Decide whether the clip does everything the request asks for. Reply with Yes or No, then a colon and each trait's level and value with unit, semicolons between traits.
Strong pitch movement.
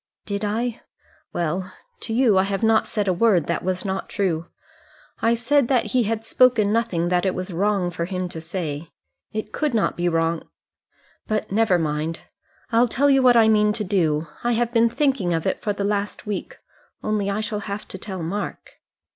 No: average, 4.2 semitones